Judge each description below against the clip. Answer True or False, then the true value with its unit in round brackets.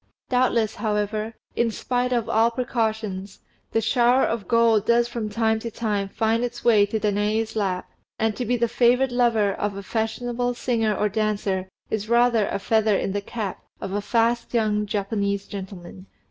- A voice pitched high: True (220 Hz)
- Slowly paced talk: False (175 wpm)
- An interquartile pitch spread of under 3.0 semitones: True (2.4 semitones)